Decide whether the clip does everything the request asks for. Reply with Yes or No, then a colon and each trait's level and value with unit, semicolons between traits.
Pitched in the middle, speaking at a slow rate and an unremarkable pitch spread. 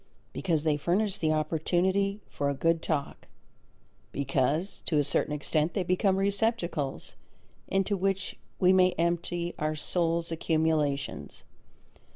Yes: medium, 170 Hz; slow, 125 wpm; average, 3.6 semitones